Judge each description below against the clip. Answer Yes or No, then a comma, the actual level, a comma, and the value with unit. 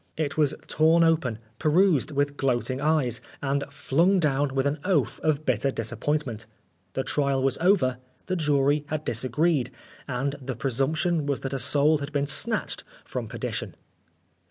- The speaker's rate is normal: Yes, average, 155 wpm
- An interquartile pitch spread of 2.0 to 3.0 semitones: Yes, average, 2.7 semitones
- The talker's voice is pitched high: No, medium, 145 Hz